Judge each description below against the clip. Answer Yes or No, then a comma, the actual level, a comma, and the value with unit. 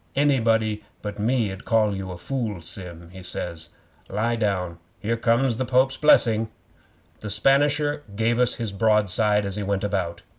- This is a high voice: No, low, 105 Hz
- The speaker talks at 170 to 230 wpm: No, average, 160 wpm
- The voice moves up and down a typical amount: Yes, average, 3.4 semitones